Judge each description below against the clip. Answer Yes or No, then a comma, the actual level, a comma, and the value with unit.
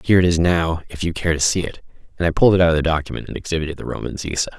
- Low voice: Yes, very low, 85 Hz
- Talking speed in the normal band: No, fast, 260 wpm